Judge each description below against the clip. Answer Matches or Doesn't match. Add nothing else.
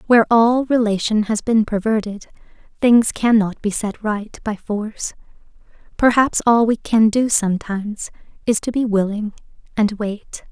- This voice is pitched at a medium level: Doesn't match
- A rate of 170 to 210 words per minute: Doesn't match